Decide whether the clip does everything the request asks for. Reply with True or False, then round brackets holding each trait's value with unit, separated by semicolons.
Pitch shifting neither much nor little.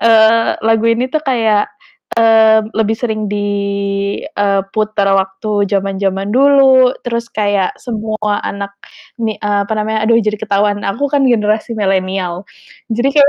False (2.2 semitones)